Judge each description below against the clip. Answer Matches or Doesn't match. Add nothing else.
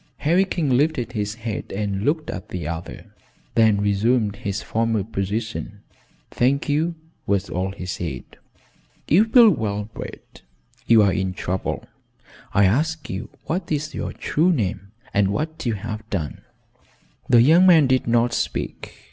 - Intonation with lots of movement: Matches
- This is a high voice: Doesn't match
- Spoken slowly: Doesn't match